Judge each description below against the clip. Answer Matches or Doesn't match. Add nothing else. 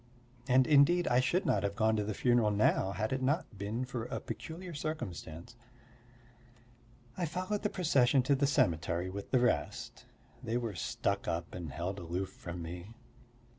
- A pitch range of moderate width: Doesn't match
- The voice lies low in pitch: Matches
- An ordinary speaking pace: Matches